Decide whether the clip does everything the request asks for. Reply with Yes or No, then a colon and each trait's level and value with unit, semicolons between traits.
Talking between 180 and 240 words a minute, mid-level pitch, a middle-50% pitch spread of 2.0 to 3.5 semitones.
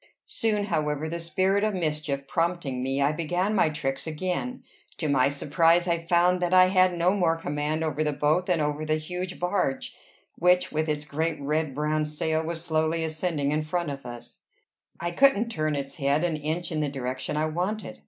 Yes: average, 195 wpm; medium, 160 Hz; average, 3.1 semitones